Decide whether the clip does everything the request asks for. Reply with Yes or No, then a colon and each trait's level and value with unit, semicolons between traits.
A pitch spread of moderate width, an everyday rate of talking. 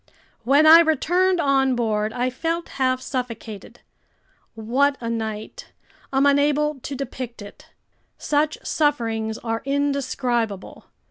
No: average, 4.0 semitones; slow, 115 wpm